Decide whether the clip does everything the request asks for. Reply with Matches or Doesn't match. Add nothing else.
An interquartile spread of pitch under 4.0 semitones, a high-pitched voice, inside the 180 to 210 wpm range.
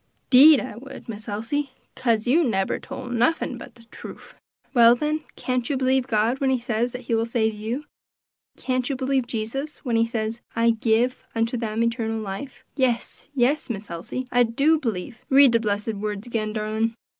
Matches